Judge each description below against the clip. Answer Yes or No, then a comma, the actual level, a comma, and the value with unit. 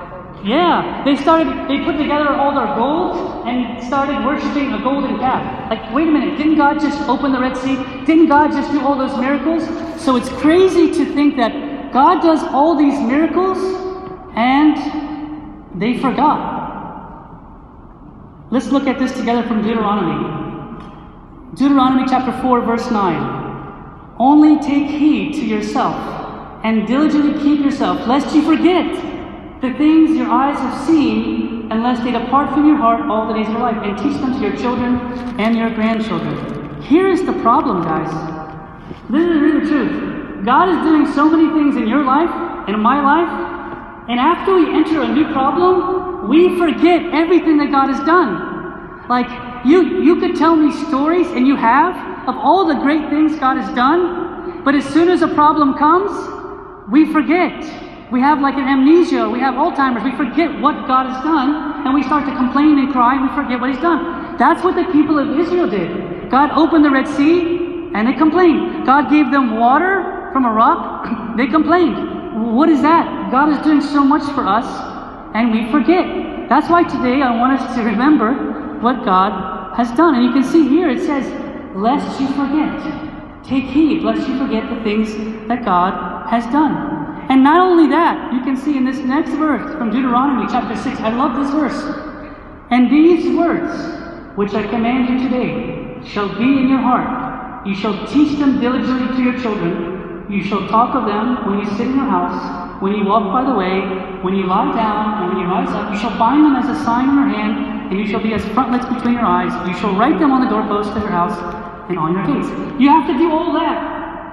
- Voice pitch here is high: Yes, very high, 280 Hz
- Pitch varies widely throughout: No, average, 4.4 semitones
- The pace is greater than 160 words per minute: Yes, average, 190 wpm